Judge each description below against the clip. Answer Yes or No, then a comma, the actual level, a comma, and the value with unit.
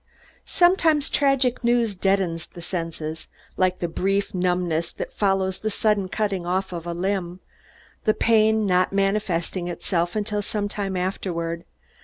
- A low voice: No, high, 190 Hz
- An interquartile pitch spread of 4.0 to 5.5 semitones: No, average, 3.2 semitones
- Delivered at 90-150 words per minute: Yes, average, 140 wpm